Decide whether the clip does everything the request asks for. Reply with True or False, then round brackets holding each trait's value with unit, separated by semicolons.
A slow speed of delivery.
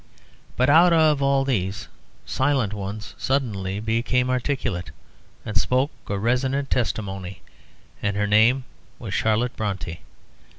True (125 wpm)